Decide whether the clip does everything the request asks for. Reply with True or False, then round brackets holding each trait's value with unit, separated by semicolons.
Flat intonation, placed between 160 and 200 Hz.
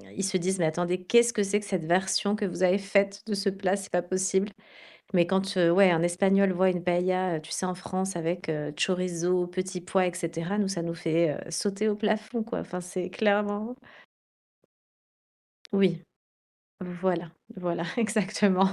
True (2.2 semitones; 185 Hz)